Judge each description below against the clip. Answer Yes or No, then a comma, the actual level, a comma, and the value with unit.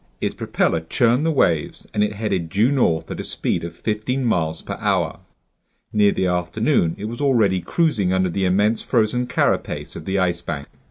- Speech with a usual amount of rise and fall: Yes, average, 4.8 semitones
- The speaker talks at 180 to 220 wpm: Yes, average, 185 wpm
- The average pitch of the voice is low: Yes, low, 100 Hz